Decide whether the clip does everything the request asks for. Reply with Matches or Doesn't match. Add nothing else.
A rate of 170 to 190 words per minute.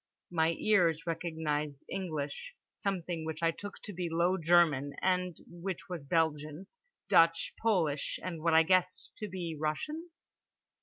Doesn't match